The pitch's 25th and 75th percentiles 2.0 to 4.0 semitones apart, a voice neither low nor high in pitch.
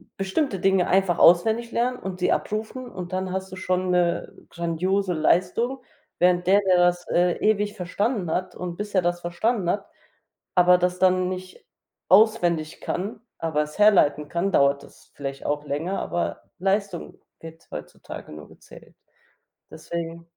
Yes: narrow, 2.4 semitones; medium, 180 Hz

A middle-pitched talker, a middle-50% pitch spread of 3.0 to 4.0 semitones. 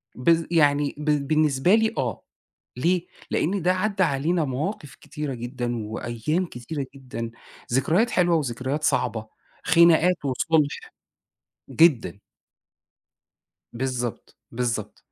No: medium, 145 Hz; average, 5.3 semitones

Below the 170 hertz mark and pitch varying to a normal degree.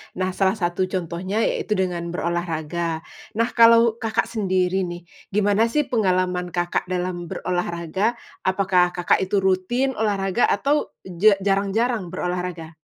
No: medium, 185 Hz; average, 3.2 semitones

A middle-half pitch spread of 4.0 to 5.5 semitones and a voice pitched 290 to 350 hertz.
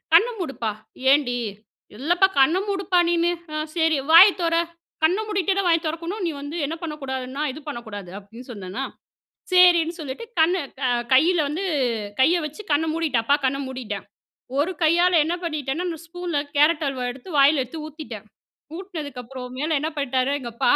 Yes: average, 4.5 semitones; very high, 310 Hz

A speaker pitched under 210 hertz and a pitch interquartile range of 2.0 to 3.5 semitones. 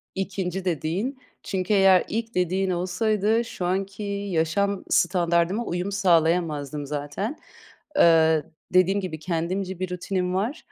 Yes: medium, 185 Hz; average, 2.7 semitones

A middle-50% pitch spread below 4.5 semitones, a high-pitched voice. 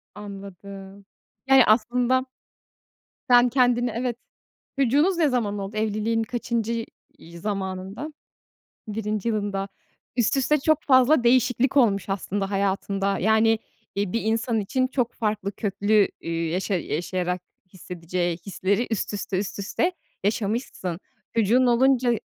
Yes: average, 3.8 semitones; high, 215 Hz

